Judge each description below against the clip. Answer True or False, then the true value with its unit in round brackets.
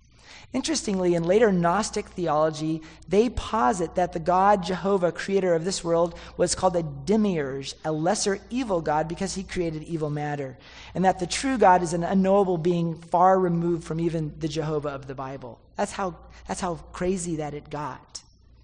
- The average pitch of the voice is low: False (175 Hz)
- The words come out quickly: False (175 wpm)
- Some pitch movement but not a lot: True (3.5 semitones)